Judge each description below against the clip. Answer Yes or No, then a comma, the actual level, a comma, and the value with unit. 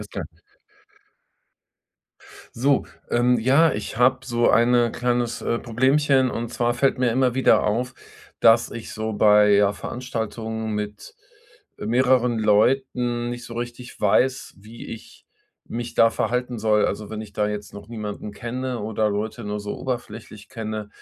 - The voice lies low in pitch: Yes, low, 115 Hz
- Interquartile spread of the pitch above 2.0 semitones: Yes, average, 2.7 semitones